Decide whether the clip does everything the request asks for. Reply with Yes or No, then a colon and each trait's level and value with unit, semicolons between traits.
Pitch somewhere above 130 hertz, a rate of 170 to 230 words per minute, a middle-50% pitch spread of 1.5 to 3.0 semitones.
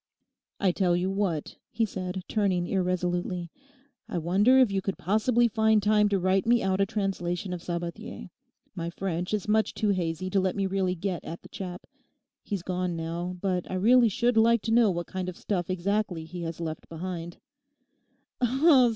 Yes: medium, 185 Hz; average, 180 wpm; average, 2.7 semitones